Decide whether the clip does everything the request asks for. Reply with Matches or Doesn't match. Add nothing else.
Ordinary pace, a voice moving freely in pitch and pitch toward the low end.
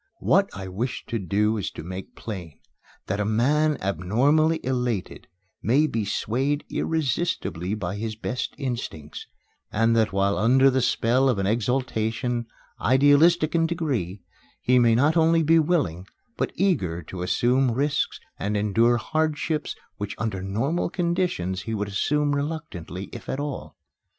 Matches